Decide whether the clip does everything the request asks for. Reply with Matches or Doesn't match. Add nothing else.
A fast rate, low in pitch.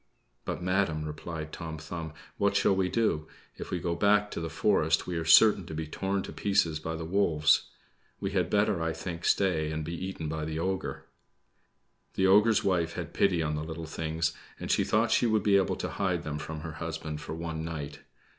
Matches